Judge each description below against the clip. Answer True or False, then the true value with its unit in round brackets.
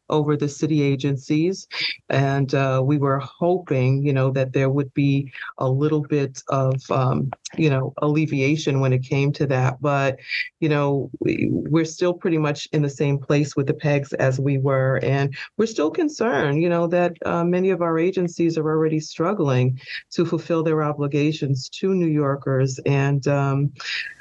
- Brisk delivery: False (175 wpm)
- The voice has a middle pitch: True (145 Hz)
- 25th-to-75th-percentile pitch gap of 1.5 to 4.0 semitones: True (2.6 semitones)